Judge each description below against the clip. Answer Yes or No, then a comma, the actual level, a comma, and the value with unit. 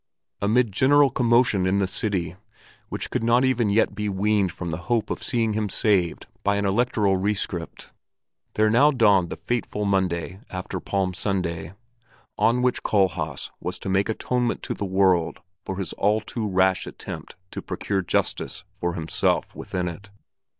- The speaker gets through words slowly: No, average, 165 wpm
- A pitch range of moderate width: Yes, average, 3.2 semitones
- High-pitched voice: No, low, 100 Hz